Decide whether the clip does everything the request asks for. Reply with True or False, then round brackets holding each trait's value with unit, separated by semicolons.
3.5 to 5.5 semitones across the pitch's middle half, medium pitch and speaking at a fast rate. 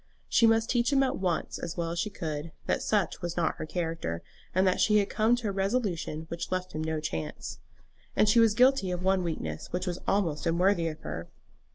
True (4.4 semitones; 180 Hz; 220 wpm)